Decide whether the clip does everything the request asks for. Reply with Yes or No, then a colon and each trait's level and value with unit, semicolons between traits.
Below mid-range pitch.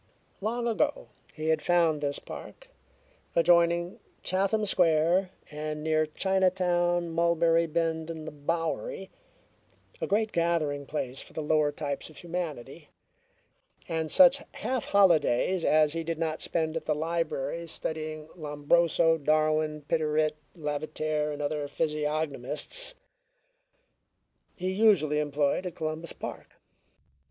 No: medium, 160 Hz